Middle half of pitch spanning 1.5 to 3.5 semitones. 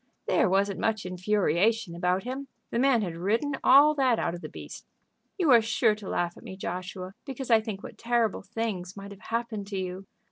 No: average, 4.1 semitones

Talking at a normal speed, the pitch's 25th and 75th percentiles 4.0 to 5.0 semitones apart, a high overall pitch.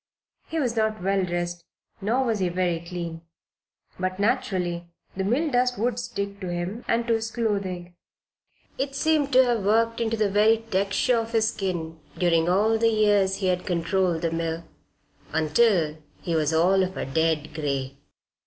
Yes: average, 170 wpm; average, 4.7 semitones; high, 195 Hz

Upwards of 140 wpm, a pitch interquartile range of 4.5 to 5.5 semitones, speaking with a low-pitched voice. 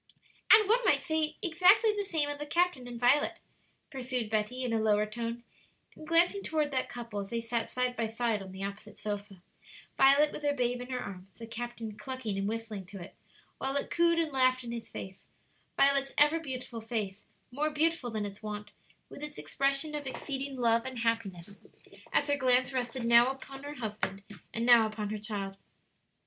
No: average, 195 wpm; average, 4.9 semitones; high, 245 Hz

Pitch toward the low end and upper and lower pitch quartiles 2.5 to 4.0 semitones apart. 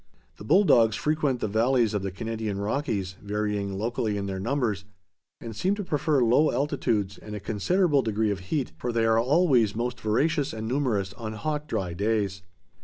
No: low, 115 Hz; average, 5.1 semitones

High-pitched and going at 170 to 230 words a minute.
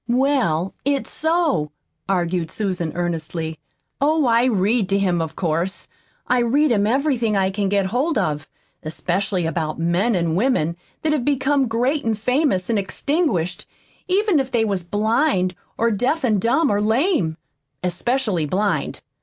No: high, 210 Hz; average, 150 wpm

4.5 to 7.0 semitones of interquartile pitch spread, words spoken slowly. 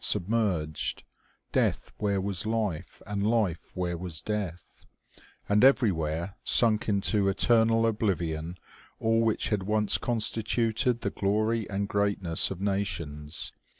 No: average, 3.8 semitones; slow, 115 wpm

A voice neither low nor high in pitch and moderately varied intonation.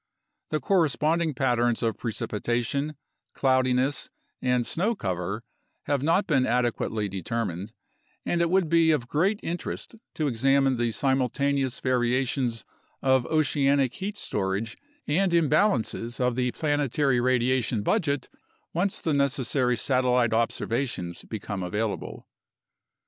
No: low, 130 Hz; average, 4.1 semitones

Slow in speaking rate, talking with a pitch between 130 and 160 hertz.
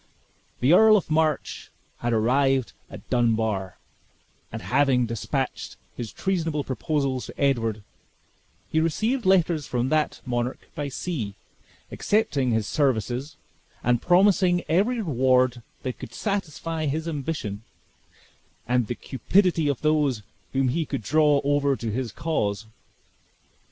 Yes: slow, 125 wpm; medium, 140 Hz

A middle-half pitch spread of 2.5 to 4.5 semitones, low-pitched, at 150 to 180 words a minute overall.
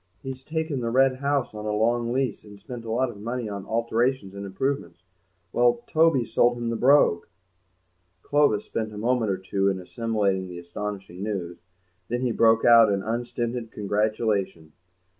Yes: average, 3.6 semitones; low, 115 Hz; average, 170 wpm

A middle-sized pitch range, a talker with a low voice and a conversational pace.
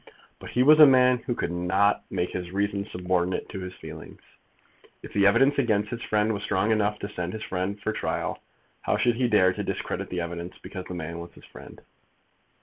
No: average, 3.4 semitones; low, 100 Hz; fast, 210 wpm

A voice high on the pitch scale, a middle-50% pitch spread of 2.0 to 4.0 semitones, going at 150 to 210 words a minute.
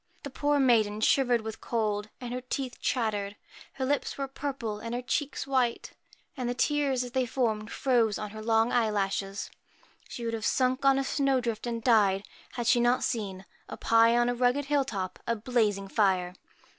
Yes: high, 240 Hz; average, 3.3 semitones; average, 195 wpm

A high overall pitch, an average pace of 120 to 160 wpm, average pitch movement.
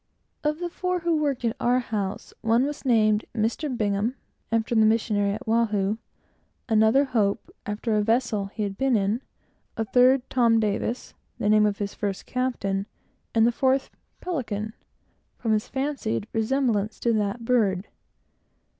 Yes: high, 225 Hz; average, 155 wpm; average, 3.3 semitones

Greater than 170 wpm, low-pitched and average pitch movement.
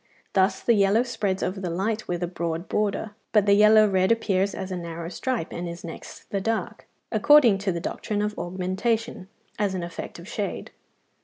No: average, 190 wpm; high, 195 Hz; average, 3.2 semitones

